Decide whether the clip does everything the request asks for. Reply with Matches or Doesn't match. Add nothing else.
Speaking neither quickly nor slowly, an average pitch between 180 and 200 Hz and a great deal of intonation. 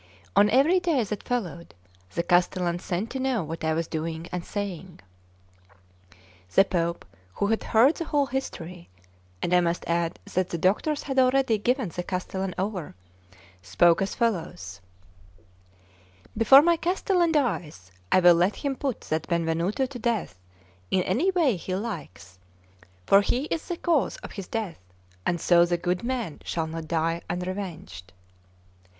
Matches